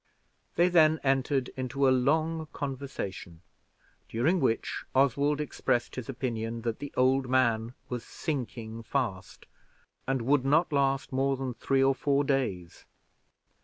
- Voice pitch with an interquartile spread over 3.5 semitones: No, average, 2.8 semitones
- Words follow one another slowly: Yes, slow, 130 wpm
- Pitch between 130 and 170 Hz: Yes, low, 135 Hz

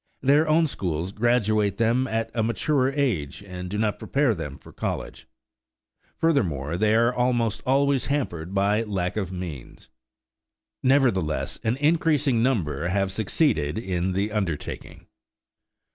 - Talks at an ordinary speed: No, slow, 130 wpm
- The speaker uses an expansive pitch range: Yes, wide, 6.2 semitones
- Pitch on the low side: Yes, low, 110 Hz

